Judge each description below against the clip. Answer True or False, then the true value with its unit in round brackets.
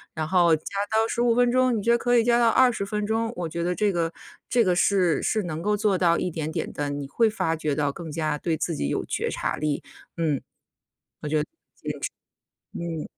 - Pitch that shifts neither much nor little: False (6.1 semitones)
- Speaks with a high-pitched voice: False (175 Hz)